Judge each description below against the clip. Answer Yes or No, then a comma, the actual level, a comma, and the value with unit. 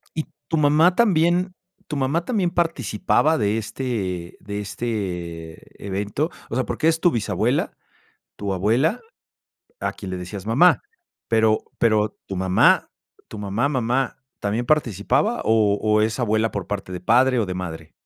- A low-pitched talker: Yes, low, 110 Hz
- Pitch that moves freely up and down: Yes, wide, 6.6 semitones